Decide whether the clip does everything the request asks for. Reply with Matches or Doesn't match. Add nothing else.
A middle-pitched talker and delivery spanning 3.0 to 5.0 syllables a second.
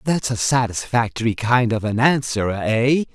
Doesn't match